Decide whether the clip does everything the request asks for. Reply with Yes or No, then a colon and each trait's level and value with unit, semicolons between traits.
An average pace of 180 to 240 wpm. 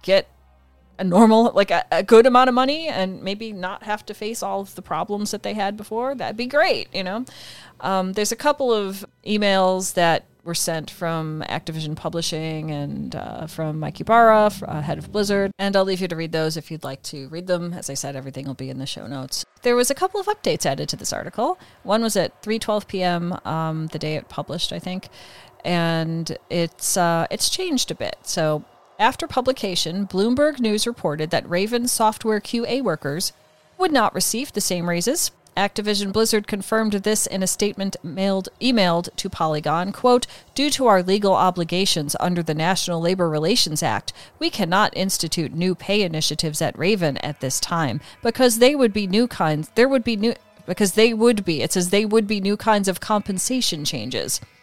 Yes: average, 195 wpm